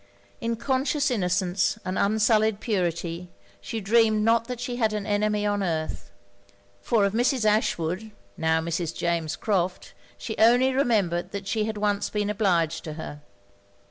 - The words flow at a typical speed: Yes, average, 150 wpm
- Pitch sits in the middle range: No, high, 205 Hz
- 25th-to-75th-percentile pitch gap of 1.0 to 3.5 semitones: No, average, 4.2 semitones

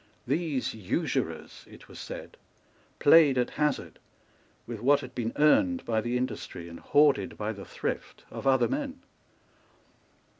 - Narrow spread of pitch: No, average, 4.4 semitones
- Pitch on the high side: No, low, 135 Hz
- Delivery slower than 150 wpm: Yes, average, 140 wpm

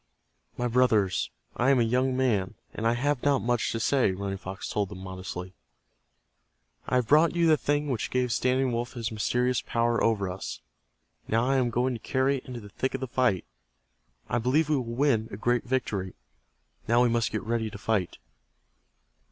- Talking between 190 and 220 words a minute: Yes, average, 195 wpm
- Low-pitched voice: Yes, low, 120 Hz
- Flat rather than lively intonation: No, average, 3.2 semitones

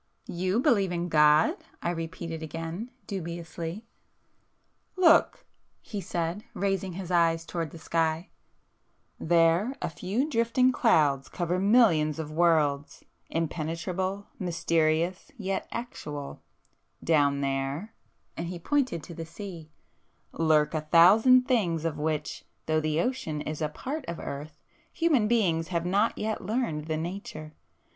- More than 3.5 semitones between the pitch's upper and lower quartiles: Yes, average, 4.1 semitones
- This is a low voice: No, medium, 170 Hz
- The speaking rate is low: Yes, slow, 125 wpm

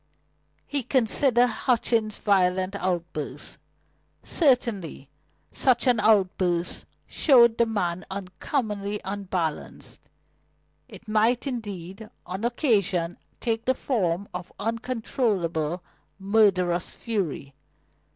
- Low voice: No, high, 205 Hz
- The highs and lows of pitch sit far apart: No, average, 4.5 semitones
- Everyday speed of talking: No, slow, 85 wpm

